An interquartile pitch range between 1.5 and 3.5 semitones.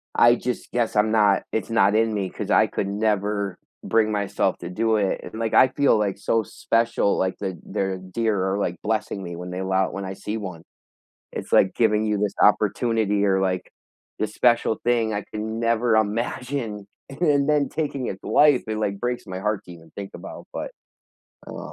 Yes: average, 2.9 semitones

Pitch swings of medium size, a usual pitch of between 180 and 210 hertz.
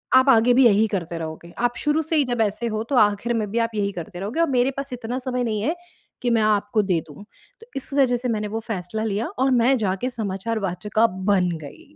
No: average, 3.8 semitones; high, 220 Hz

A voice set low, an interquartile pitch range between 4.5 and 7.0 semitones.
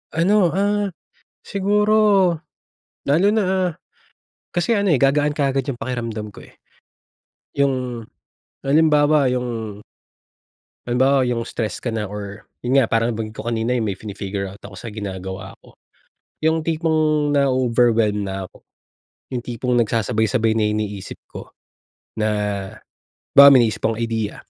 Yes: low, 125 Hz; wide, 5.5 semitones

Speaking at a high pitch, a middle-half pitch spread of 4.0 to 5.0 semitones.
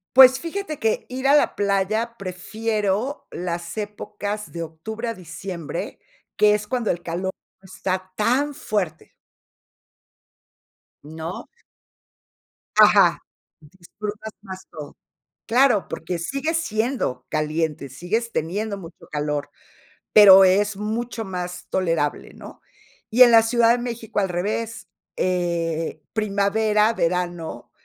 Yes: high, 200 Hz; average, 4.6 semitones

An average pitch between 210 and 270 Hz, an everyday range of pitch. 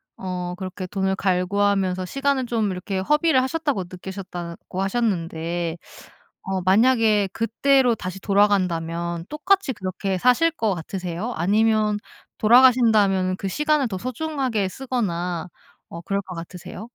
No: high, 195 Hz; average, 4.8 semitones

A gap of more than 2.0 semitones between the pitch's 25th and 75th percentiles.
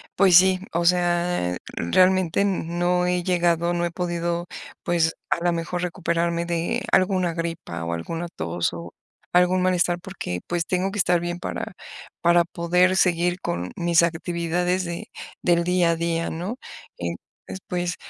No: narrow, 1.2 semitones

